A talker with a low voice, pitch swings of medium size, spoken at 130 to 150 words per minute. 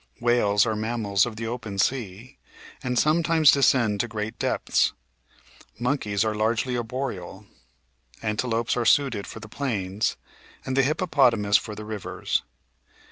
Yes: low, 115 Hz; average, 3.3 semitones; slow, 135 wpm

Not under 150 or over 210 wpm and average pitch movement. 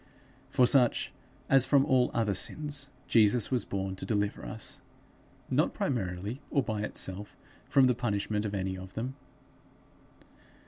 No: average, 140 wpm; average, 4.6 semitones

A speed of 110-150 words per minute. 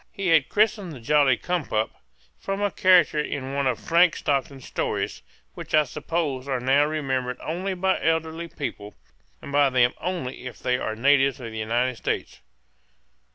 No: average, 175 wpm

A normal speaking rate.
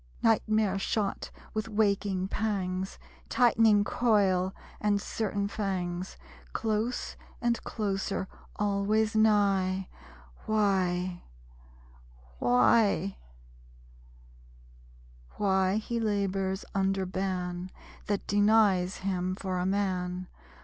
No: slow, 80 wpm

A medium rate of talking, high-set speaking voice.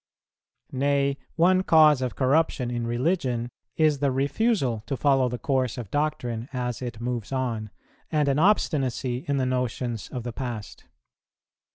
No: average, 150 wpm; low, 130 Hz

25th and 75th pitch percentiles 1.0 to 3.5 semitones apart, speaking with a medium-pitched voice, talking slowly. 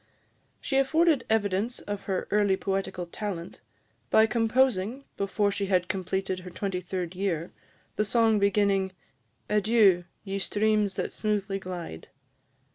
No: narrow, 2.5 semitones; high, 200 Hz; slow, 125 wpm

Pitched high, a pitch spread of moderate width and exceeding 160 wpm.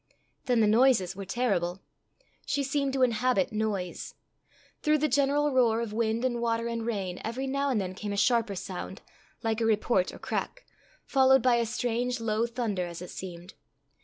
Yes: high, 230 Hz; average, 4.0 semitones; average, 180 wpm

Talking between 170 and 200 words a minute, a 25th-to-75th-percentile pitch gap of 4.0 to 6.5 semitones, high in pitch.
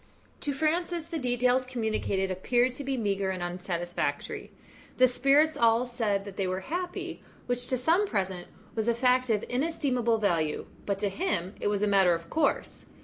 Yes: average, 175 wpm; average, 5.3 semitones; high, 235 Hz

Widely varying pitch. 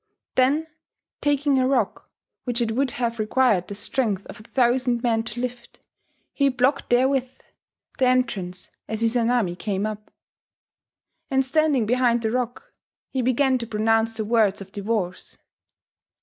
No: average, 2.9 semitones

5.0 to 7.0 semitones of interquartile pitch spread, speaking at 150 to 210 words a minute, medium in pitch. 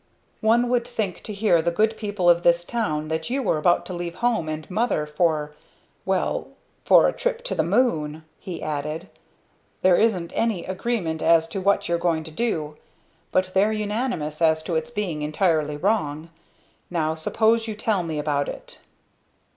Yes: wide, 5.6 semitones; average, 175 wpm; medium, 175 Hz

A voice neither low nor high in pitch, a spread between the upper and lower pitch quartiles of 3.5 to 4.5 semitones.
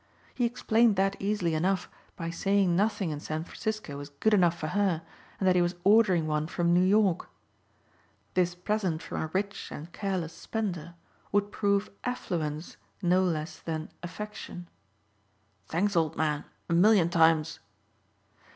Yes: medium, 180 Hz; average, 3.8 semitones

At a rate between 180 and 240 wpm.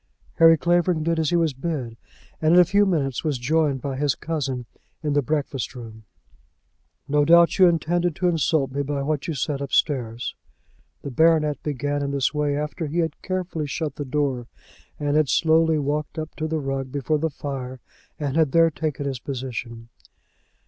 Yes: average, 185 wpm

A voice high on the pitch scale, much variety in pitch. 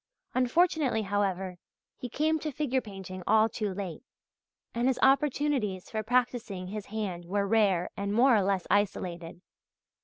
No: high, 210 Hz; average, 4.9 semitones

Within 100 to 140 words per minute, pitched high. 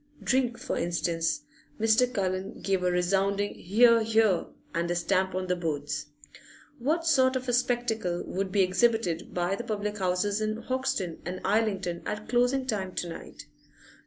No: average, 160 wpm; high, 200 Hz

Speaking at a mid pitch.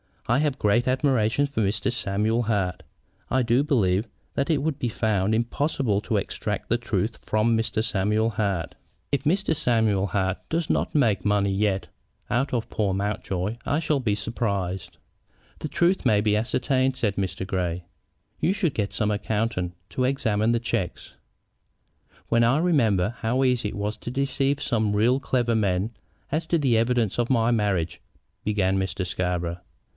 No: low, 110 Hz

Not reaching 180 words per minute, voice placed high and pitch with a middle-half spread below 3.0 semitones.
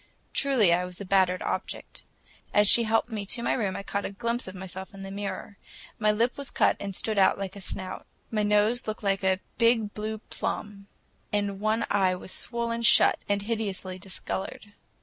No: average, 195 wpm; high, 205 Hz; narrow, 2.4 semitones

